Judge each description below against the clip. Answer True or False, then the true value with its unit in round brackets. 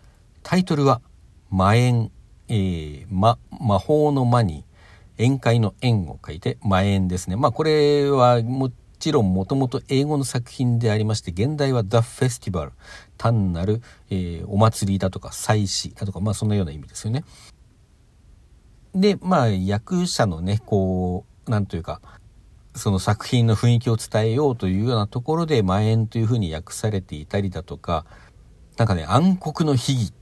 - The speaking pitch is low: True (110 Hz)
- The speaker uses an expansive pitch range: False (4.6 semitones)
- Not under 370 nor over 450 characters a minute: False (330 characters per minute)